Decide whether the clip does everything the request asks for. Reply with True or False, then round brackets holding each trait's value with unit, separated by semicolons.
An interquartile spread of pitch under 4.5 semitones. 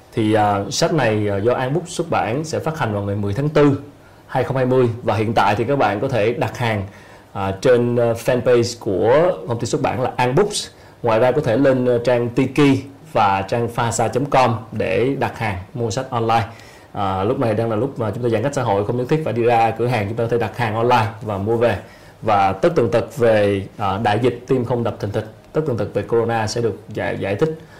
True (2.8 semitones)